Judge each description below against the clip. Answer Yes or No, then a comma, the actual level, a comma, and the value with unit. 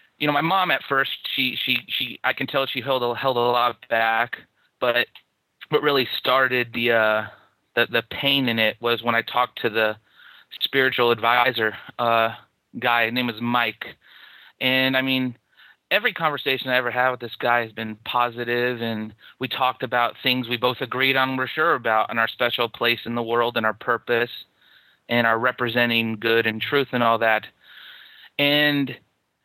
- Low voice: Yes, low, 120 Hz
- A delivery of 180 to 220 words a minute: Yes, average, 185 wpm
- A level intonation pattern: Yes, narrow, 2.0 semitones